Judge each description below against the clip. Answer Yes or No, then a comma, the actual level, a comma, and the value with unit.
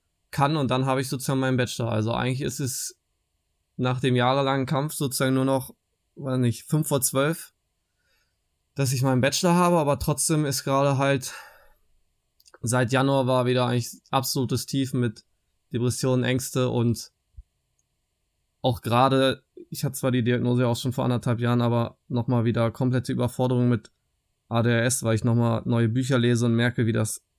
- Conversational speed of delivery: Yes, average, 160 wpm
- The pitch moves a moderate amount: No, narrow, 2.2 semitones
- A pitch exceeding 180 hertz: No, low, 125 Hz